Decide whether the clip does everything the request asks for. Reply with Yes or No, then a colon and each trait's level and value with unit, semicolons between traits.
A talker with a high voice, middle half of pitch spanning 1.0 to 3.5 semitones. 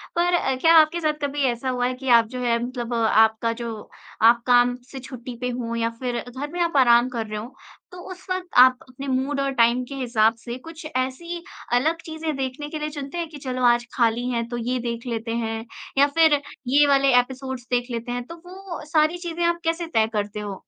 No: very high, 255 Hz; average, 4.3 semitones